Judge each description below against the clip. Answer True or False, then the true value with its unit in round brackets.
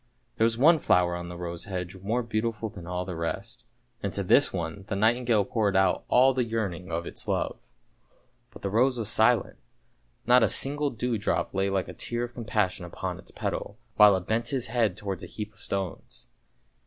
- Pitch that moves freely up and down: False (4.2 semitones)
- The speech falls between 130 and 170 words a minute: False (205 wpm)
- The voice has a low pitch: True (105 Hz)